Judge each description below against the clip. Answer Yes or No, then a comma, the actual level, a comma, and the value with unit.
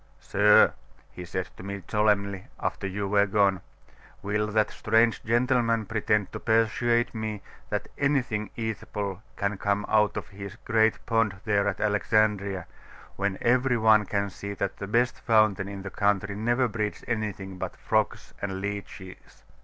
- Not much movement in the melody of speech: Yes, narrow, 1.9 semitones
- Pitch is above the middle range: No, low, 105 Hz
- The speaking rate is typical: Yes, average, 155 wpm